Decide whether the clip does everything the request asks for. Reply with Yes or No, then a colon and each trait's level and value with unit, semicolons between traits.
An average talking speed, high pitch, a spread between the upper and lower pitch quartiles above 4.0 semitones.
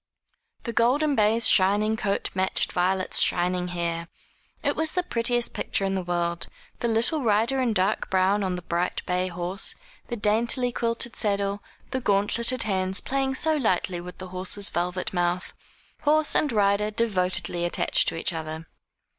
Yes: average, 160 wpm; high, 200 Hz; average, 4.4 semitones